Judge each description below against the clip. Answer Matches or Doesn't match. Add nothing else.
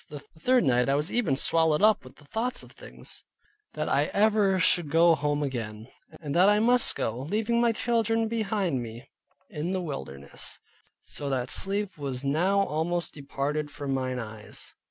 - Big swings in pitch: Matches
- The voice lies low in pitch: Doesn't match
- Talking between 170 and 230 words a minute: Matches